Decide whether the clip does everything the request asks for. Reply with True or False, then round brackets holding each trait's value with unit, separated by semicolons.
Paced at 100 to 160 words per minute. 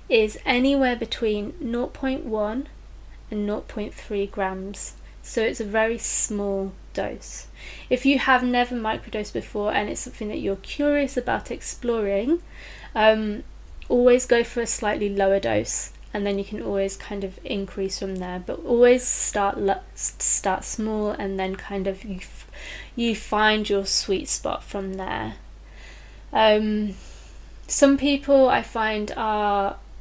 True (140 wpm)